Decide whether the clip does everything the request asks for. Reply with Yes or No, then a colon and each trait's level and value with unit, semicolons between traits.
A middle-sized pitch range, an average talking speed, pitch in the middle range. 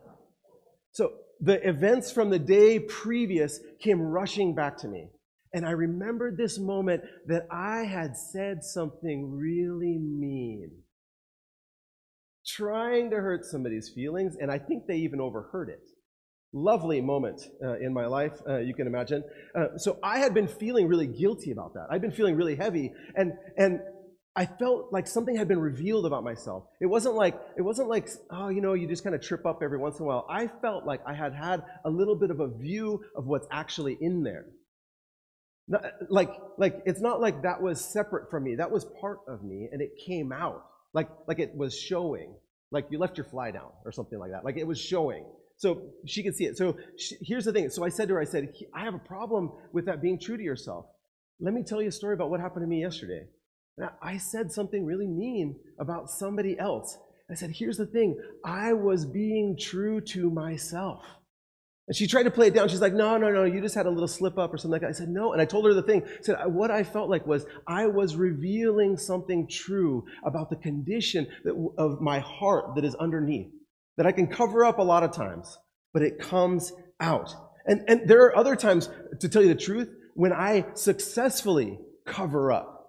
No: average, 4.9 semitones; fast, 210 wpm; medium, 180 Hz